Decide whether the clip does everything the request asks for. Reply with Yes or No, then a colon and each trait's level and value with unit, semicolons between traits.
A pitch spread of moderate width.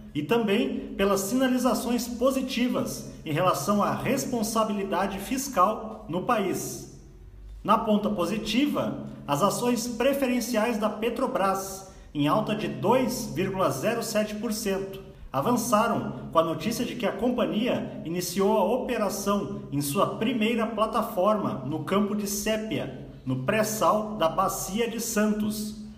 Yes: average, 3.4 semitones